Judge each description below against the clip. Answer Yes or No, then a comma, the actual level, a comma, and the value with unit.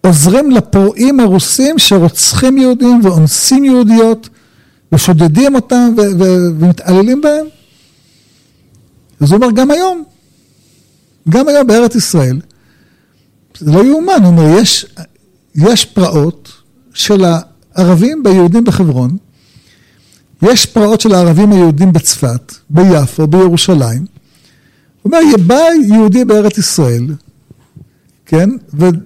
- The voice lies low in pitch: No, medium, 185 Hz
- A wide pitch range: Yes, wide, 6.7 semitones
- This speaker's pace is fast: No, average, 105 wpm